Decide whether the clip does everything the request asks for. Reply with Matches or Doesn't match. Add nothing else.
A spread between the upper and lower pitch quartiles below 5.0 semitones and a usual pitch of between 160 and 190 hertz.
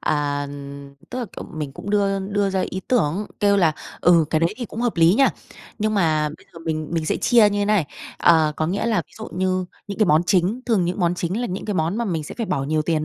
Matches